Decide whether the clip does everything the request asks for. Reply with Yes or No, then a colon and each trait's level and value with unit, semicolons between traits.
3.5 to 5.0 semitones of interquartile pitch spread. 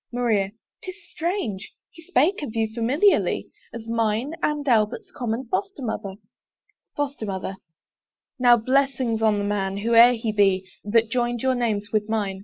Yes: average, 3.9 semitones